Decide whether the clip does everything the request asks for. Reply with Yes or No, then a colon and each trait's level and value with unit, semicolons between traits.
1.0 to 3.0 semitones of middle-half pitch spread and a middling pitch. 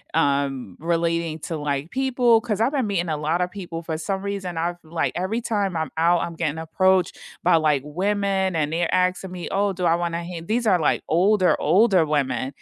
No: average, 3.4 semitones; medium, 175 Hz